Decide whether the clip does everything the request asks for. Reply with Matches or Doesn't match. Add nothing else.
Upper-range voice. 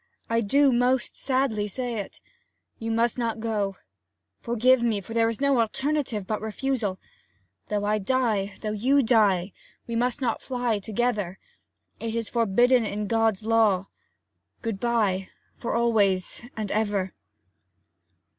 Matches